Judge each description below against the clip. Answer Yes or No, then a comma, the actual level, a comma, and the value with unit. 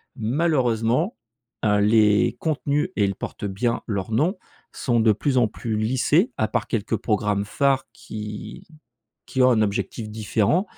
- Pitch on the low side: Yes, low, 115 Hz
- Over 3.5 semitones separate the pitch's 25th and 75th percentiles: Yes, average, 4.1 semitones